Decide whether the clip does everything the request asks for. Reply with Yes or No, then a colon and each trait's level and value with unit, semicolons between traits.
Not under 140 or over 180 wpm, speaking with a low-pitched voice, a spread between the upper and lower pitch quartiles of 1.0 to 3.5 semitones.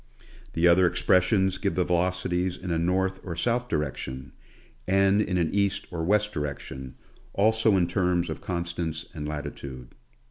Yes: average, 155 wpm; very low, 90 Hz; average, 2.8 semitones